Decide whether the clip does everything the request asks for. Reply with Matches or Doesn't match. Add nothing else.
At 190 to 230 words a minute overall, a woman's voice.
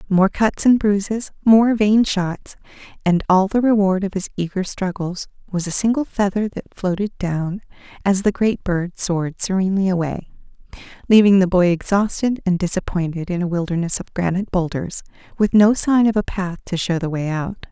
Doesn't match